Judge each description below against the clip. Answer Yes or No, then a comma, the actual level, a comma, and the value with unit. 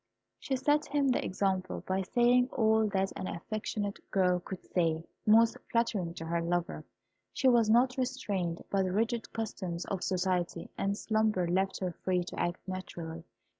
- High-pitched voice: Yes, high, 195 Hz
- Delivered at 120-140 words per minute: No, average, 165 wpm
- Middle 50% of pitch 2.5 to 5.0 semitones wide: Yes, average, 4.2 semitones